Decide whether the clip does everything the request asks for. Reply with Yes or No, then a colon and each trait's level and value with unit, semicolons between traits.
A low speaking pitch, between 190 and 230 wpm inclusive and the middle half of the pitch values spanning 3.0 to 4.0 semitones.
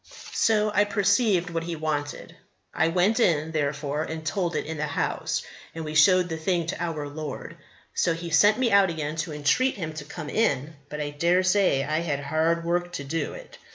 No: medium, 165 Hz; fast, 205 wpm; average, 3.3 semitones